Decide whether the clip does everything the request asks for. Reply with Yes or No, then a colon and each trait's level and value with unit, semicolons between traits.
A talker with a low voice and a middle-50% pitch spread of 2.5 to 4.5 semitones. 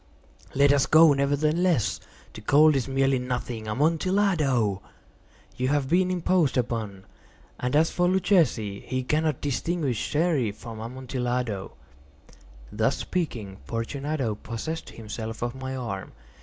No: low, 130 Hz; average, 5.3 semitones